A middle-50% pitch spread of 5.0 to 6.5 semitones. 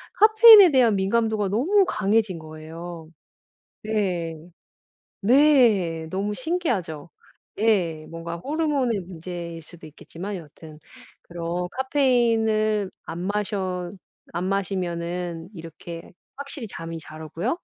Yes: average, 5.3 semitones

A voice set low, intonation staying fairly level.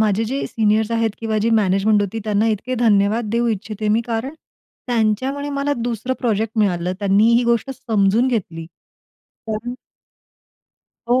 No: high, 220 Hz; narrow, 2.3 semitones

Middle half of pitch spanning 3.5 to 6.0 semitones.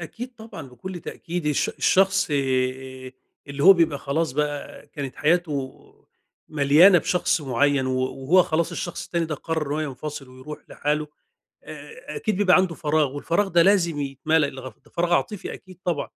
Yes: average, 4.0 semitones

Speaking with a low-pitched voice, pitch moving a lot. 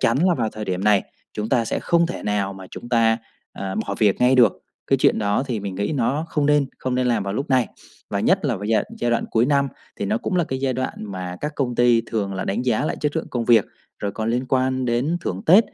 No: low, 120 Hz; average, 4.4 semitones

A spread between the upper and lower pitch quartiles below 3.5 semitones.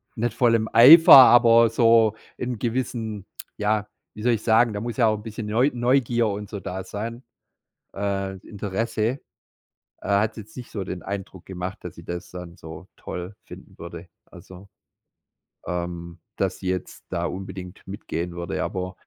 No: average, 3.8 semitones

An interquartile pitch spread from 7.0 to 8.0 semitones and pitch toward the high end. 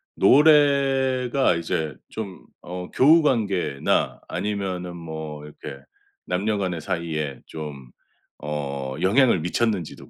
No: wide, 7.3 semitones; very low, 90 Hz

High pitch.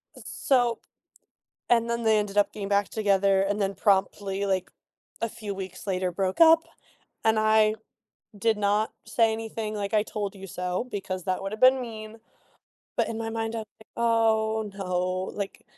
Yes: high, 210 Hz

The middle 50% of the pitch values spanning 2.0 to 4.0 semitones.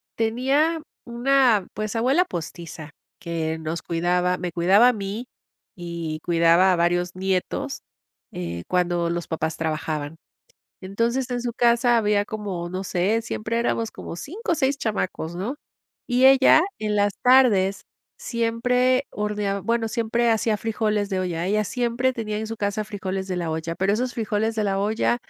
No: average, 5.0 semitones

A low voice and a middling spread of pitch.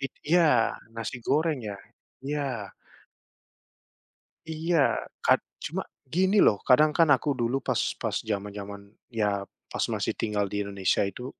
No: low, 120 Hz; wide, 6.5 semitones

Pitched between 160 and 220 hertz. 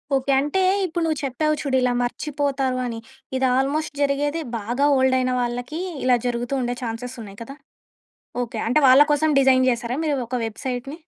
No: very high, 260 Hz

